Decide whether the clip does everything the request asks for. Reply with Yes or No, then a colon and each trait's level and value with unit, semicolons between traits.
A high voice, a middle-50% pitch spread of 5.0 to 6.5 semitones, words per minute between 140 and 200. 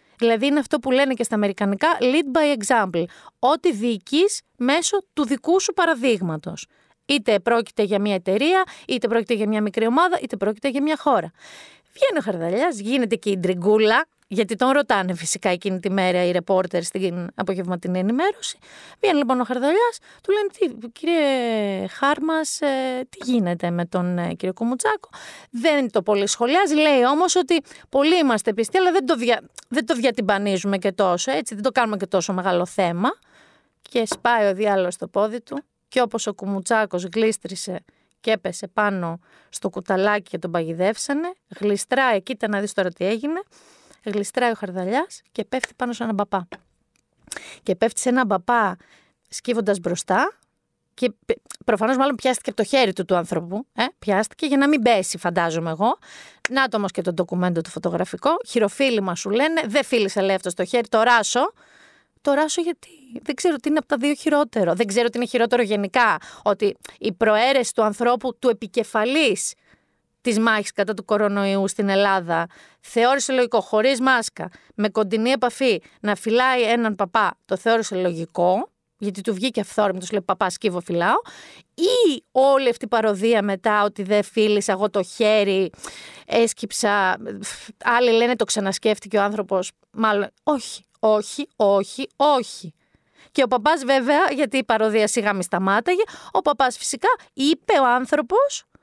Yes: high, 225 Hz; average, 5.3 semitones; average, 160 wpm